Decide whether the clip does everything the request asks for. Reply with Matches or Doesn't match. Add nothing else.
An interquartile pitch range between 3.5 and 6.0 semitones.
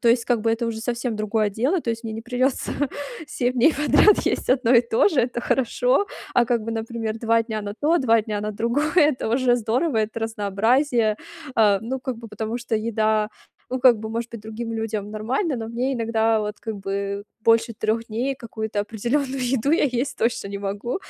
Doesn't match